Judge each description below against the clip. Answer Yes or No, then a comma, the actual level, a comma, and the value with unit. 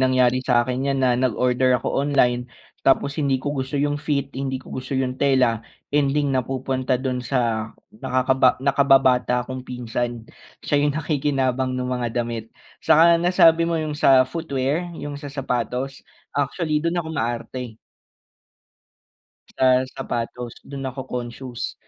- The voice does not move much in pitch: Yes, narrow, 2.3 semitones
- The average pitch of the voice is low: Yes, low, 130 Hz